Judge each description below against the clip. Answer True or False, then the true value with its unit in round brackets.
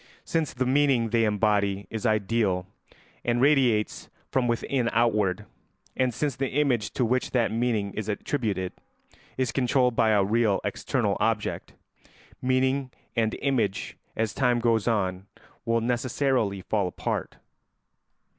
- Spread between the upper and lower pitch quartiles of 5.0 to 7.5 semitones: False (3.4 semitones)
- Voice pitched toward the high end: False (115 Hz)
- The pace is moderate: False (130 wpm)